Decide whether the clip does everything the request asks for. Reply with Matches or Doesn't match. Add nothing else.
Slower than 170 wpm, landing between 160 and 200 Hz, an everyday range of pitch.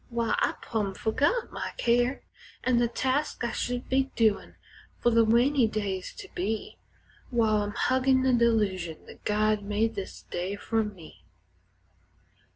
Doesn't match